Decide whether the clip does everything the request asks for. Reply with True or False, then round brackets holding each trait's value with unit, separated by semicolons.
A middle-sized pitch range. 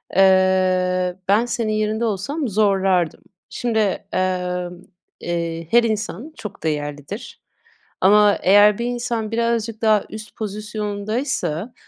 True (3.4 semitones)